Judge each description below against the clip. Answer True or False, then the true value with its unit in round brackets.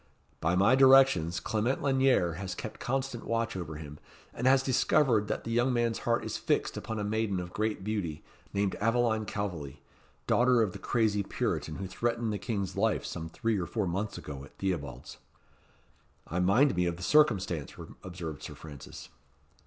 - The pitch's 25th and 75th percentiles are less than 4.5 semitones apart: False (5.1 semitones)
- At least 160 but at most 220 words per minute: True (175 wpm)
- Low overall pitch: True (105 Hz)